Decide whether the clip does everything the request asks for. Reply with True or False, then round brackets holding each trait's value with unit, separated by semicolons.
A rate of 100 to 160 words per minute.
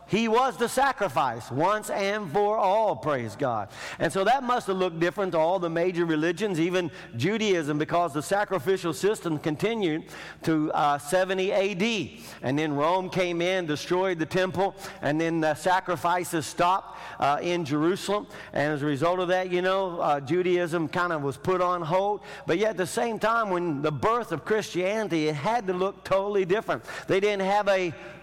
False (185 wpm)